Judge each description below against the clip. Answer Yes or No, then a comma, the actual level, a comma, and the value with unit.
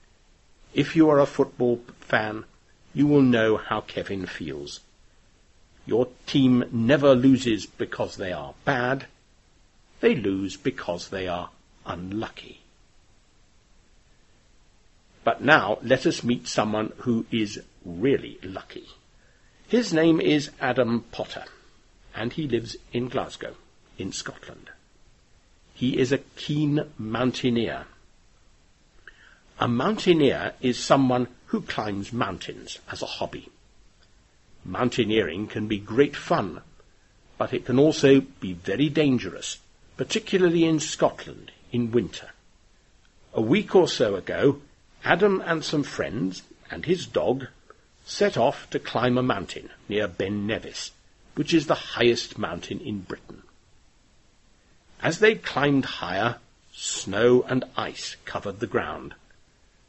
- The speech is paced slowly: Yes, slow, 120 wpm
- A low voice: Yes, low, 120 Hz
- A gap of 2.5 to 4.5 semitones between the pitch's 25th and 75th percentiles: No, average, 5.2 semitones